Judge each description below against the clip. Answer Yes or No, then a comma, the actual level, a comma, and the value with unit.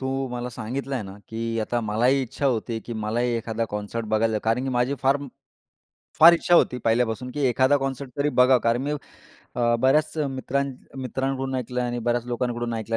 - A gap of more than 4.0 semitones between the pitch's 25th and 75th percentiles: No, average, 2.7 semitones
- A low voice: Yes, low, 120 Hz